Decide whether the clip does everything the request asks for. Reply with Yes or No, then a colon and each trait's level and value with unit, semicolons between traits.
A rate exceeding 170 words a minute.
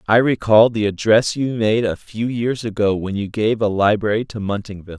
Yes: fast, 205 wpm